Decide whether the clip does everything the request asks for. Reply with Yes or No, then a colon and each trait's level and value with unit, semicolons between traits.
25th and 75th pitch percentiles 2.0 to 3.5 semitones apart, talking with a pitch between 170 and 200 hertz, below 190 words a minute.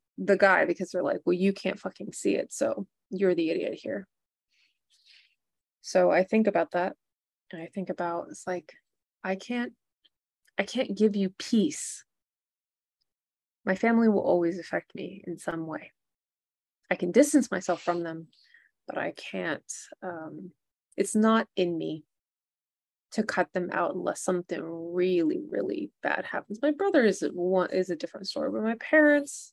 No: average, 3.9 semitones; medium, 185 Hz; average, 160 wpm